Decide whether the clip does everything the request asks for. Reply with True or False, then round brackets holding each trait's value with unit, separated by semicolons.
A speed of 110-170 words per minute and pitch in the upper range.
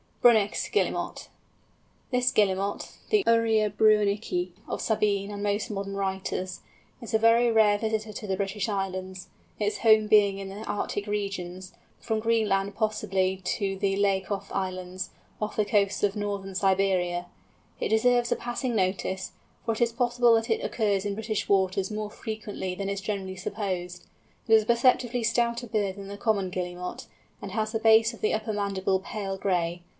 True (165 wpm; 205 Hz)